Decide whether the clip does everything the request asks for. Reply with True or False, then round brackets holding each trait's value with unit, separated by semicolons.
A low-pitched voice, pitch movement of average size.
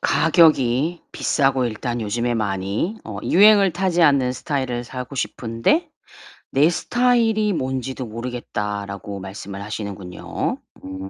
False (125 Hz; 7.9 semitones)